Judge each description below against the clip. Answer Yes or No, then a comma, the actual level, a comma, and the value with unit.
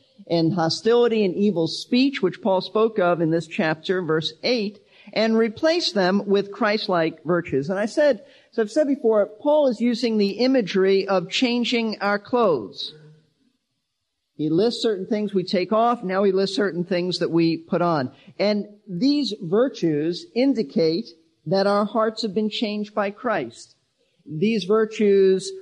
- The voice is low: No, high, 205 Hz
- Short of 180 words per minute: Yes, average, 155 wpm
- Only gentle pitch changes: No, average, 4.2 semitones